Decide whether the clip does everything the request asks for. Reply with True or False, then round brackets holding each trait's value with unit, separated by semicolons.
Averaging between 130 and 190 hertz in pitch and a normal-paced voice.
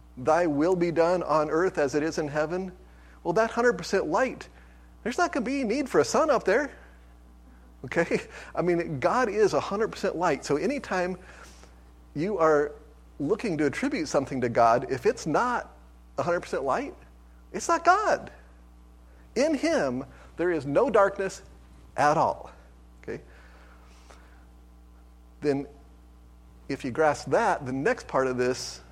False (115 Hz; 145 wpm)